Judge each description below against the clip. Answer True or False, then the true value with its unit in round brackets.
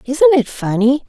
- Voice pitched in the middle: False (255 Hz)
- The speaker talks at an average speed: True (165 wpm)